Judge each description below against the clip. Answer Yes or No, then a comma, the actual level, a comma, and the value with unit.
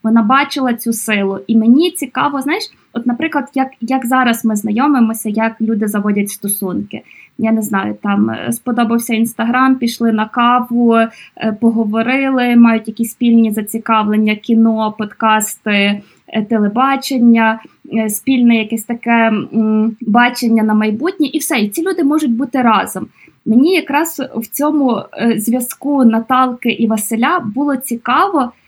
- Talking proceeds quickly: No, average, 125 wpm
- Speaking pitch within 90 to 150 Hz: No, high, 230 Hz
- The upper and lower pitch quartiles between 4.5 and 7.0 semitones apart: No, average, 2.9 semitones